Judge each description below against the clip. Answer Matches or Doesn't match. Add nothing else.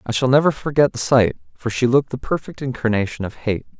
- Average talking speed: Doesn't match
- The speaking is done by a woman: Doesn't match